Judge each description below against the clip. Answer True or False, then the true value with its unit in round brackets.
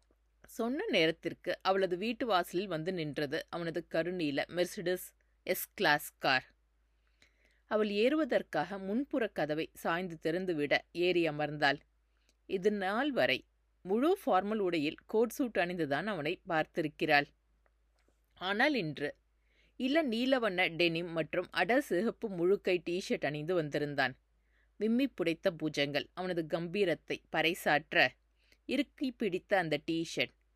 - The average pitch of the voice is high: False (175 Hz)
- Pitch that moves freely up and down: True (5.7 semitones)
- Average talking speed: True (100 wpm)